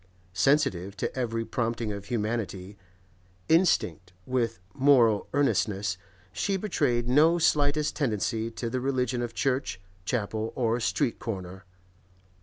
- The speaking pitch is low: Yes, low, 115 Hz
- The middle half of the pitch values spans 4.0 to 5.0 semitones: Yes, average, 4.4 semitones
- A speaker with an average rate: No, slow, 115 wpm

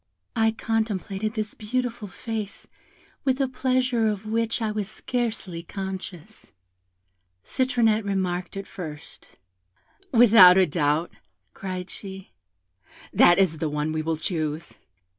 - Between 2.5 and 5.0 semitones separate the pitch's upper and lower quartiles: Yes, average, 4.1 semitones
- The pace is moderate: No, slow, 120 wpm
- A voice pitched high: Yes, high, 200 Hz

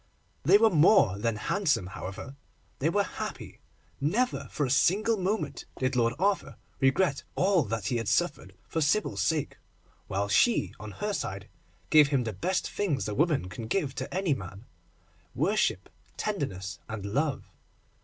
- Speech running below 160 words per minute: Yes, average, 150 wpm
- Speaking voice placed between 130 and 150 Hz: Yes, medium, 140 Hz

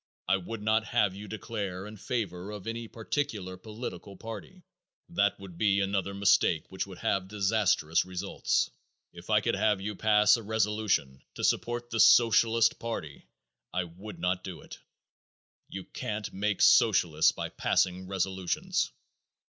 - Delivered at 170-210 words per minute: No, average, 150 wpm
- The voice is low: Yes, low, 100 Hz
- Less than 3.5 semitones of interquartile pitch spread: Yes, average, 2.9 semitones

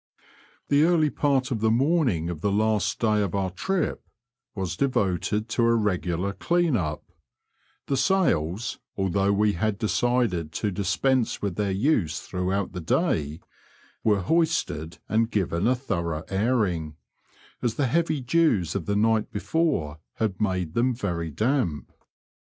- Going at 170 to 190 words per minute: No, average, 145 wpm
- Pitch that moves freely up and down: Yes, wide, 5.9 semitones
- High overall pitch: No, low, 105 Hz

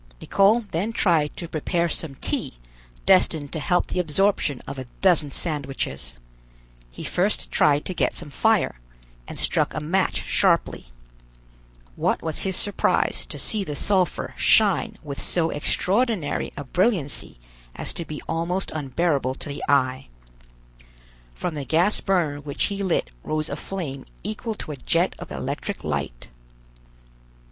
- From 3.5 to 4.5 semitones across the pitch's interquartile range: No, average, 5.0 semitones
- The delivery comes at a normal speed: Yes, average, 145 wpm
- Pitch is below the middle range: No, medium, 165 Hz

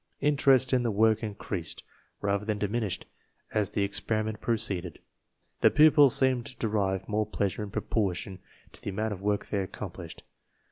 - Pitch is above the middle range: No, low, 105 Hz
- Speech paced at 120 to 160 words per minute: Yes, average, 155 wpm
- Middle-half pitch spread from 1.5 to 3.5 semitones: Yes, average, 2.9 semitones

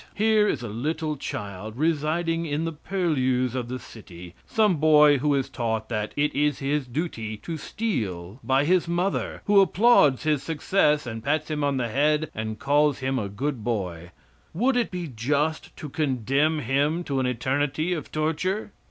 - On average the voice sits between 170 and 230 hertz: No, medium, 145 Hz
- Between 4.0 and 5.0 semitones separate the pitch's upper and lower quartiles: Yes, average, 4.7 semitones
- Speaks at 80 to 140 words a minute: No, average, 175 wpm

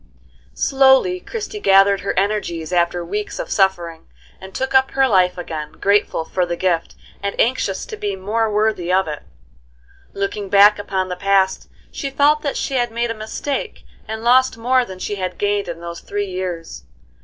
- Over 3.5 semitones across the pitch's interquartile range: Yes, average, 4.6 semitones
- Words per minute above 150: Yes, average, 180 wpm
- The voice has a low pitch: No, high, 200 Hz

